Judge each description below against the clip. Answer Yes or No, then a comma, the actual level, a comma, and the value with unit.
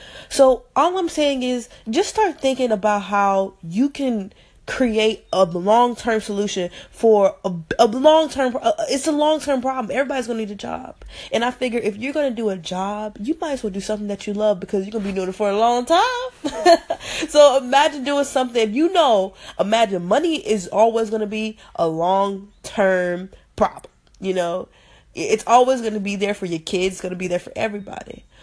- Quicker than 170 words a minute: Yes, average, 200 wpm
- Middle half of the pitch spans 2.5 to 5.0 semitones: No, wide, 5.4 semitones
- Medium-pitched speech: No, high, 225 Hz